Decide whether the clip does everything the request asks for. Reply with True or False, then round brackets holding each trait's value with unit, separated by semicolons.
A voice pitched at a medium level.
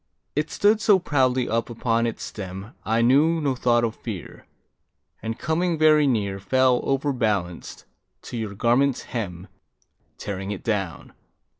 False (120 Hz)